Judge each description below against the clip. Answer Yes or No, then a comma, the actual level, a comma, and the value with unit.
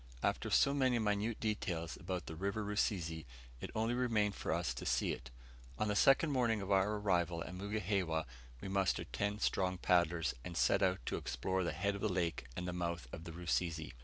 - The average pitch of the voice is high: No, very low, 95 Hz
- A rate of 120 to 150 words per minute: No, average, 200 wpm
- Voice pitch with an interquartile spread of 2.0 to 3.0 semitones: No, average, 3.5 semitones